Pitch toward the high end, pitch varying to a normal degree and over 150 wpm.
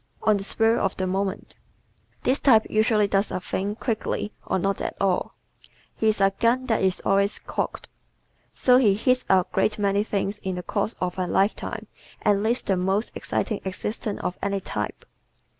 No: high, 200 Hz; narrow, 2.3 semitones; average, 185 wpm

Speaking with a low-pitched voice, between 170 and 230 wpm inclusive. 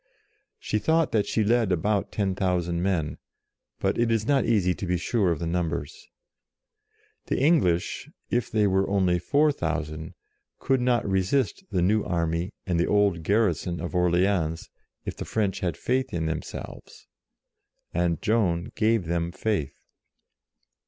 No: very low, 95 Hz; average, 155 wpm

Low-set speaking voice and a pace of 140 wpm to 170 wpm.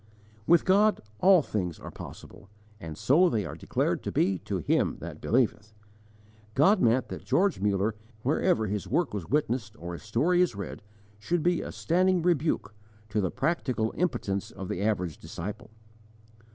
Yes: low, 115 Hz; average, 165 wpm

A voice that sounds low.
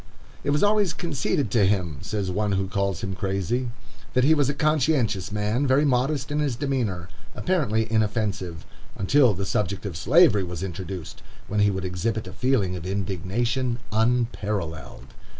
Yes: low, 105 Hz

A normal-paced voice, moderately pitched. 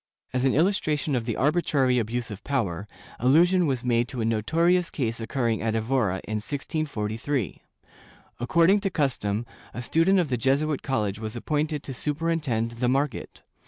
No: average, 165 wpm; low, 130 Hz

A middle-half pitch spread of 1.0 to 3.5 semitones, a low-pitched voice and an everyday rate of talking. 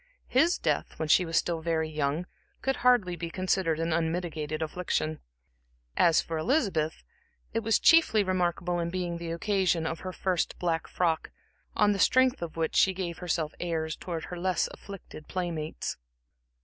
No: narrow, 2.6 semitones; medium, 175 Hz; average, 160 wpm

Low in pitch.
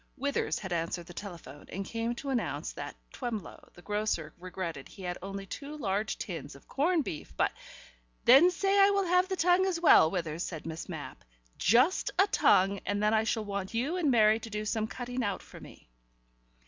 No: high, 215 Hz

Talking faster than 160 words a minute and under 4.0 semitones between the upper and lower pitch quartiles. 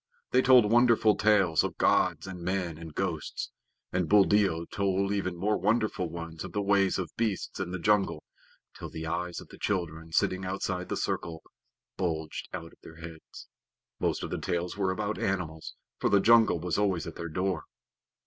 Yes: average, 180 wpm; average, 3.4 semitones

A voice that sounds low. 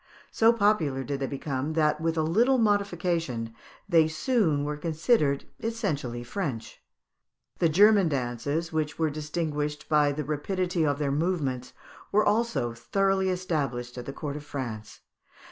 No: medium, 155 Hz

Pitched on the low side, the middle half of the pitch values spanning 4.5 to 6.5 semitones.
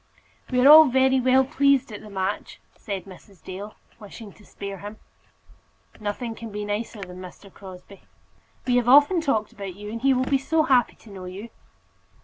No: high, 215 Hz; average, 4.8 semitones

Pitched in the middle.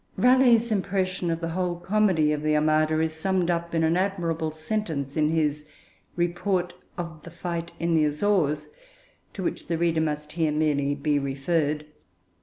Yes: medium, 165 Hz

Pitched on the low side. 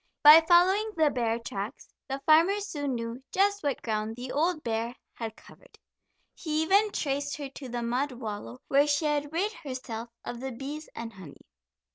No: very high, 275 Hz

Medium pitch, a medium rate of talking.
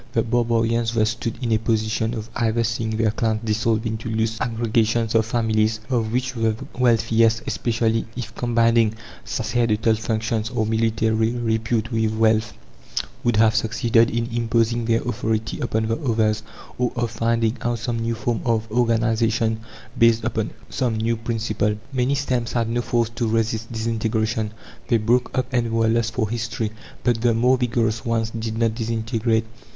No: low, 115 Hz; average, 160 wpm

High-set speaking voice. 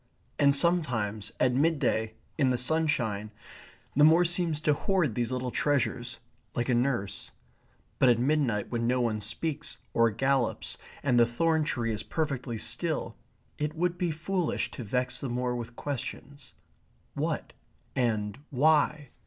No: low, 130 Hz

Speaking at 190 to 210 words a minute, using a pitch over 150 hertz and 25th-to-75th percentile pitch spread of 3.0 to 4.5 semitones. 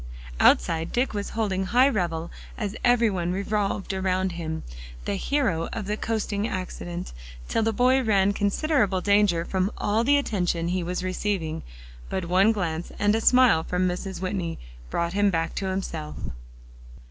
No: average, 160 wpm; high, 190 Hz; average, 3.5 semitones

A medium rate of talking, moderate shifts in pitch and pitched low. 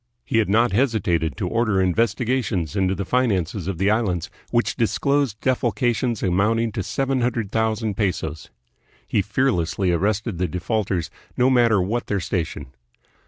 Yes: average, 150 wpm; average, 4.3 semitones; low, 105 Hz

